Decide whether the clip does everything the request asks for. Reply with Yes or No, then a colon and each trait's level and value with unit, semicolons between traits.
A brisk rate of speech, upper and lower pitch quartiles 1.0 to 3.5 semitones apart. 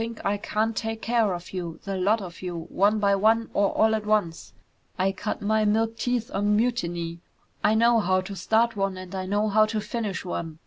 Yes: fast, 220 wpm; average, 2.9 semitones